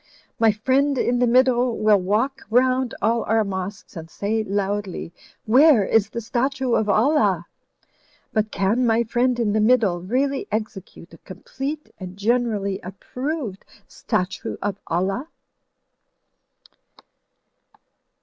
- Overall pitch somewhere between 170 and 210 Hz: No, high, 220 Hz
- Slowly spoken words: Yes, slow, 120 wpm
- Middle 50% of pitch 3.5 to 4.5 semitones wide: Yes, average, 4.2 semitones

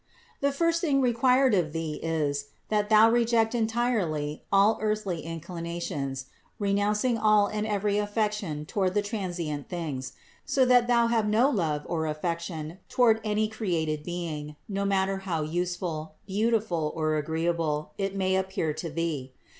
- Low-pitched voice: No, high, 190 Hz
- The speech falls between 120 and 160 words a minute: Yes, average, 145 wpm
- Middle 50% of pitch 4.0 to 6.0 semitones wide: Yes, average, 5.3 semitones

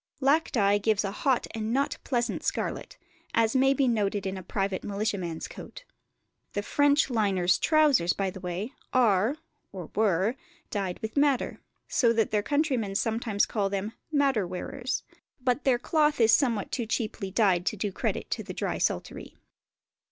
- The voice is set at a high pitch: Yes, high, 220 Hz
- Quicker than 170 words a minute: No, average, 165 wpm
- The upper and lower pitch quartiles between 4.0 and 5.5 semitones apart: Yes, average, 4.9 semitones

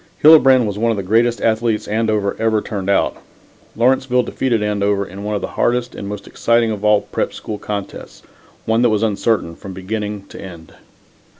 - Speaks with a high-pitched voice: No, low, 105 Hz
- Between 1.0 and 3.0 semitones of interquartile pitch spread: Yes, narrow, 2.5 semitones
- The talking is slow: No, average, 185 wpm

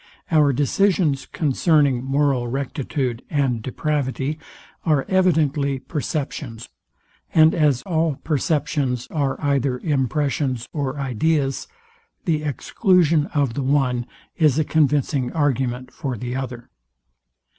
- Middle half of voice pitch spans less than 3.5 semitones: Yes, average, 2.9 semitones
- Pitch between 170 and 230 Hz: No, medium, 140 Hz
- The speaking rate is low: Yes, slow, 105 wpm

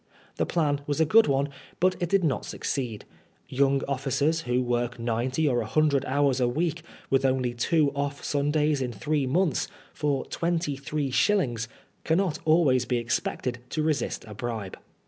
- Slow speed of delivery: No, average, 165 wpm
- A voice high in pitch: No, medium, 140 Hz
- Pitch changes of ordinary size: Yes, average, 3.7 semitones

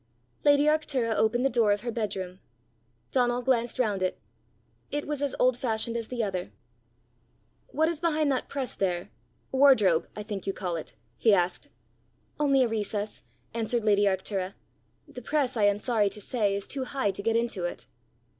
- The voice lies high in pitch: Yes, high, 230 Hz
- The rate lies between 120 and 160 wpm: No, average, 175 wpm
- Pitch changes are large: No, average, 4.5 semitones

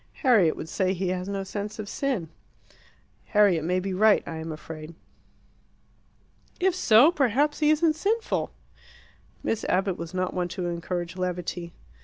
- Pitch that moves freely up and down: No, average, 4.9 semitones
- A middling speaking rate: Yes, average, 150 wpm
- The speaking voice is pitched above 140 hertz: Yes, high, 190 Hz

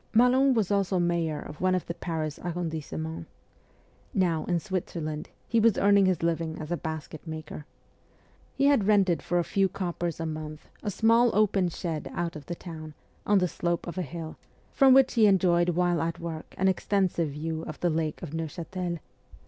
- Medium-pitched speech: Yes, medium, 175 Hz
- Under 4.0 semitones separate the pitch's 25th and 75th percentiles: Yes, average, 3.1 semitones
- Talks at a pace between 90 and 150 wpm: No, average, 185 wpm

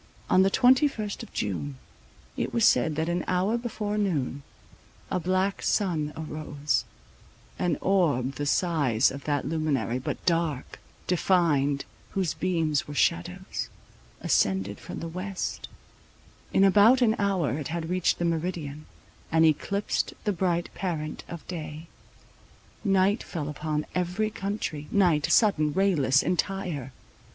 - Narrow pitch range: No, average, 4.5 semitones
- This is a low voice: No, medium, 170 Hz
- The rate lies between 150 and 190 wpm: No, slow, 135 wpm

